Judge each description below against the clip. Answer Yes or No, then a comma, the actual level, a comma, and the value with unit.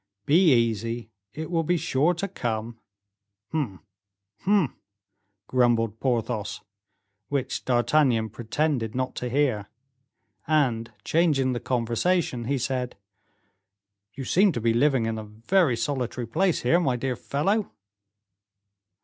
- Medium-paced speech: No, slow, 120 wpm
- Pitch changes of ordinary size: Yes, average, 4.9 semitones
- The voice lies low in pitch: Yes, low, 125 Hz